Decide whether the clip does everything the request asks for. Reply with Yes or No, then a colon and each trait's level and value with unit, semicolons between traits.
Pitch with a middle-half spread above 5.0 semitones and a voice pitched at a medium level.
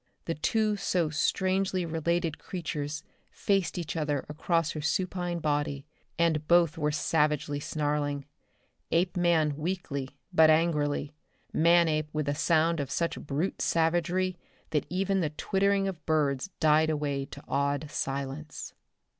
No: average, 2.8 semitones; medium, 160 Hz